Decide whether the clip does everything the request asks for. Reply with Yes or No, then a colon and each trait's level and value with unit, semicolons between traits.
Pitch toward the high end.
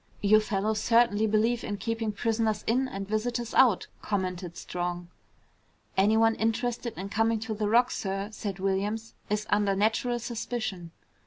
Yes: high, 215 Hz